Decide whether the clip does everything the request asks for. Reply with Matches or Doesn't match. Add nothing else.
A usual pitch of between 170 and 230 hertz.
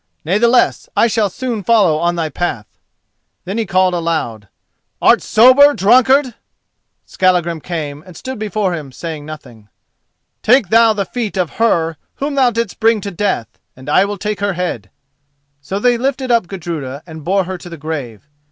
Matches